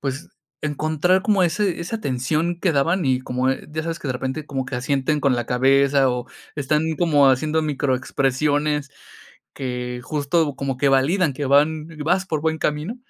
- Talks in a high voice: No, medium, 145 Hz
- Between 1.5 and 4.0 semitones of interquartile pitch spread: Yes, average, 3.1 semitones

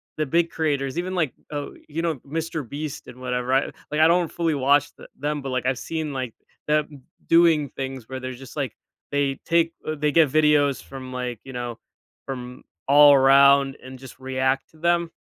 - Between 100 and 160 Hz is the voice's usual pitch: Yes, medium, 140 Hz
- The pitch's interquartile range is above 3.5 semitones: No, average, 2.9 semitones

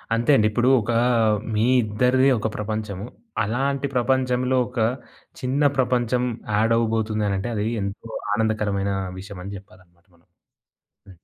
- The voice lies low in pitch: Yes, low, 110 Hz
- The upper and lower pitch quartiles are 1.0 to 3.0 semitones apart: No, average, 3.6 semitones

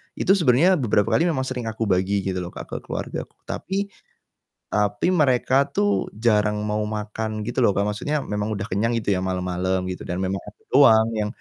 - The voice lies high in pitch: No, low, 105 Hz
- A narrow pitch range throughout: No, average, 3.7 semitones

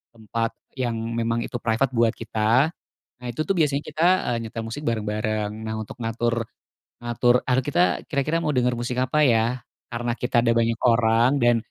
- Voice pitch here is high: No, low, 120 Hz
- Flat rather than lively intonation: Yes, narrow, 1.9 semitones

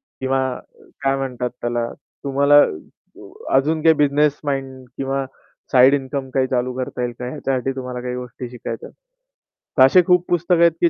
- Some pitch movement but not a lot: No, narrow, 2.3 semitones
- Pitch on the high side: No, low, 135 Hz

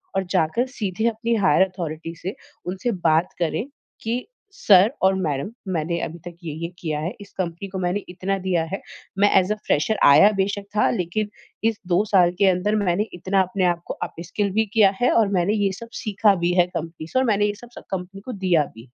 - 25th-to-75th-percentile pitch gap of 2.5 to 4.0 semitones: Yes, average, 3.2 semitones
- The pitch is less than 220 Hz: Yes, medium, 185 Hz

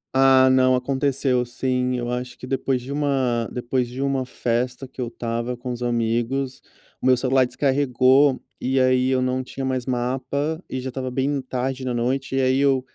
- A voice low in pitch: Yes, low, 130 Hz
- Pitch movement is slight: Yes, narrow, 1.3 semitones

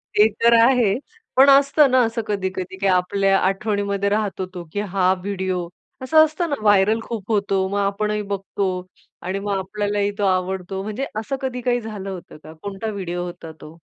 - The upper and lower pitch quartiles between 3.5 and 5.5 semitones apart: No, average, 2.7 semitones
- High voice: Yes, high, 200 Hz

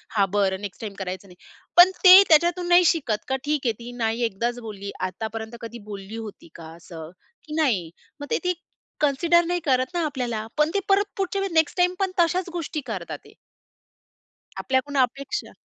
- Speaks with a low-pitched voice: No, very high, 260 Hz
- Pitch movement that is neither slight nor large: No, wide, 8.4 semitones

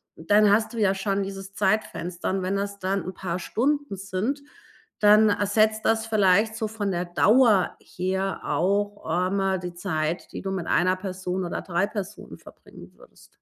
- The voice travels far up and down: No, narrow, 2.4 semitones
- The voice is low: No, high, 195 Hz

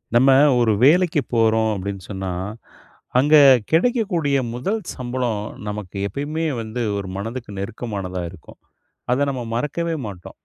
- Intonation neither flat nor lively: No, wide, 6.2 semitones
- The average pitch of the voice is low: Yes, low, 120 Hz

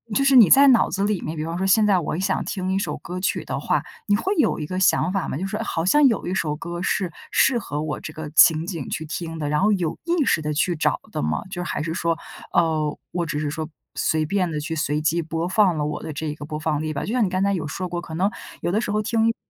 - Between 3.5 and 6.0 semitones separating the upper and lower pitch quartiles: Yes, average, 4.0 semitones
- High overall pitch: No, medium, 170 Hz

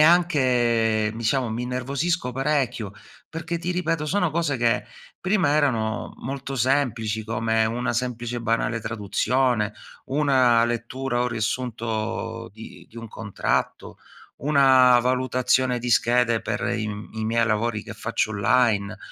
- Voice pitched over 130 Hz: No, low, 120 Hz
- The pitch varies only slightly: No, average, 3.1 semitones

